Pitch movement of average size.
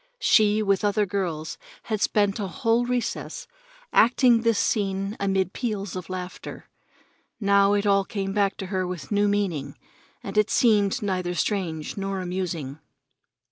No: narrow, 2.2 semitones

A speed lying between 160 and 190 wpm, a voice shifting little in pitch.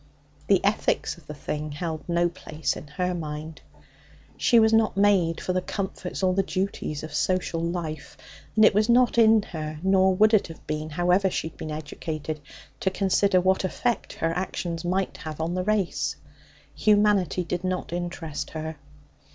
No: average, 175 wpm; average, 3.5 semitones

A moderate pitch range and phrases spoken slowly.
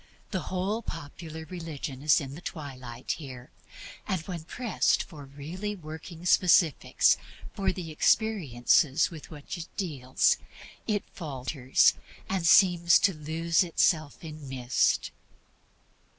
Yes: average, 4.0 semitones; slow, 120 wpm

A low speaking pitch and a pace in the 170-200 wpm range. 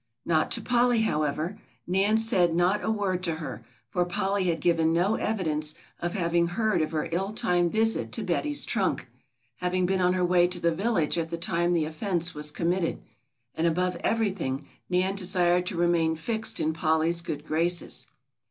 No: medium, 175 Hz; average, 180 wpm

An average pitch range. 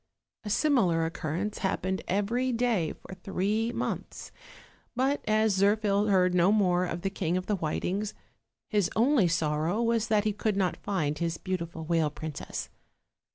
Yes: average, 4.0 semitones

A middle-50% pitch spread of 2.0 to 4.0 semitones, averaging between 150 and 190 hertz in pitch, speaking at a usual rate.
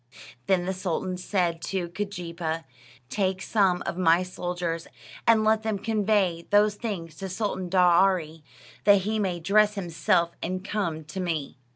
Yes: average, 3.1 semitones; medium, 185 Hz; average, 150 wpm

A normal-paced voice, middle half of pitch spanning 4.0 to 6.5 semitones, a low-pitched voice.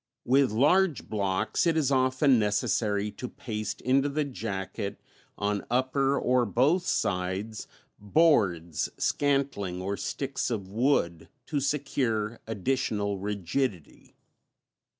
No: slow, 110 wpm; average, 5.3 semitones; low, 115 Hz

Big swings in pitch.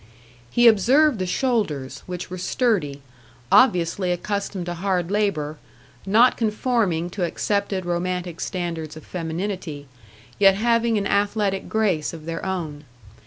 No: average, 3.9 semitones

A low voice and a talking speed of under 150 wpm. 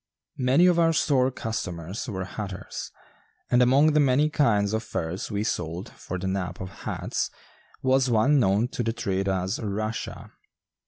No: low, 110 Hz; average, 160 wpm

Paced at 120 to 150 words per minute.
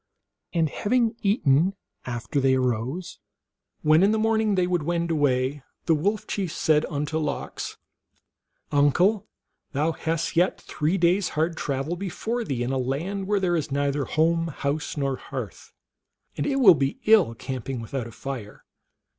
No: average, 160 wpm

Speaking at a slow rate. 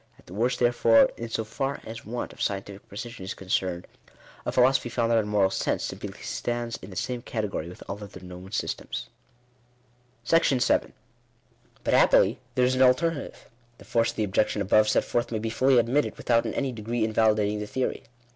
No: average, 195 wpm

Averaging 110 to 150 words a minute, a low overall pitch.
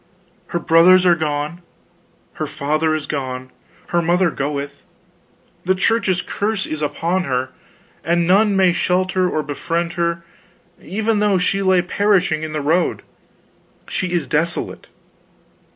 No: slow, 135 wpm; medium, 170 Hz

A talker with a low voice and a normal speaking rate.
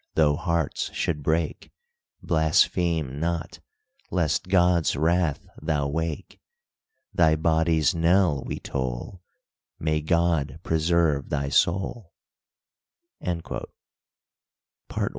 No: very low, 80 Hz; slow, 90 wpm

